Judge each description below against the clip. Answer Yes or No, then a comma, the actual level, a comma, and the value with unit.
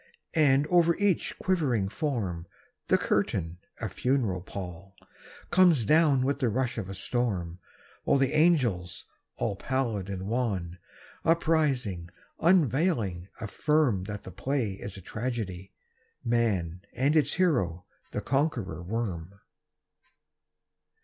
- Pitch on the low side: Yes, low, 115 Hz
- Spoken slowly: Yes, slow, 115 wpm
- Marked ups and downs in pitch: Yes, wide, 7.1 semitones